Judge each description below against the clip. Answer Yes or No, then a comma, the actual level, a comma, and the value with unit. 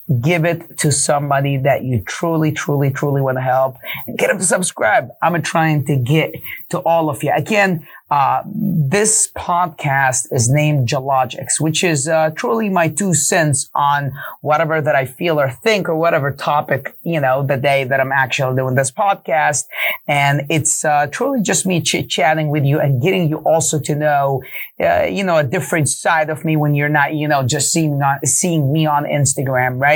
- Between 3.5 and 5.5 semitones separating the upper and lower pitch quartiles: No, average, 2.9 semitones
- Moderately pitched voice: Yes, medium, 150 Hz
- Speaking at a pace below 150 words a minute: No, average, 190 wpm